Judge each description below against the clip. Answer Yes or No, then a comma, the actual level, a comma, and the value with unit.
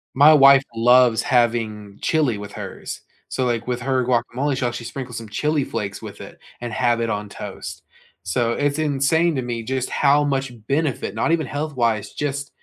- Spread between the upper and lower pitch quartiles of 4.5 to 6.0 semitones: No, average, 3.3 semitones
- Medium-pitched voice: No, low, 125 Hz